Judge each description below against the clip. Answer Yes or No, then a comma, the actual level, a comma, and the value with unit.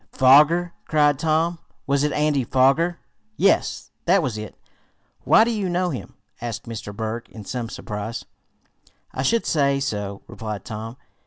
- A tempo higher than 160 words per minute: No, average, 150 wpm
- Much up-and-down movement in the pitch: Yes, wide, 6.4 semitones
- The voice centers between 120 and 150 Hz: Yes, low, 135 Hz